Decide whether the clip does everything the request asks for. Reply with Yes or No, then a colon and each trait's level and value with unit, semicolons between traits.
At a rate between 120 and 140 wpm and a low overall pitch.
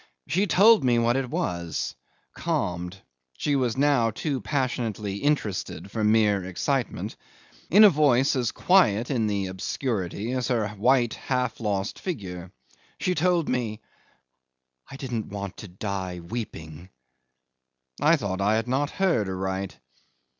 Yes: slow, 135 wpm; low, 115 Hz